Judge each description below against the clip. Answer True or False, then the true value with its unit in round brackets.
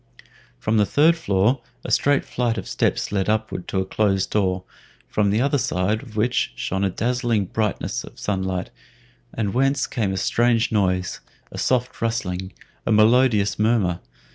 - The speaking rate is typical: True (165 wpm)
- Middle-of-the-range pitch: False (105 Hz)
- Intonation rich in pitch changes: False (3.8 semitones)